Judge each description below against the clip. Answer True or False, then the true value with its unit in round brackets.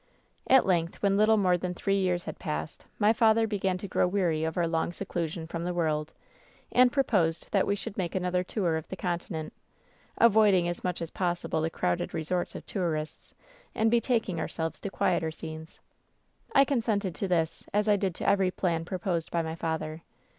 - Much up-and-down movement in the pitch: False (3.5 semitones)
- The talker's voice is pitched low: False (180 Hz)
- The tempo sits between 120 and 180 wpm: False (195 wpm)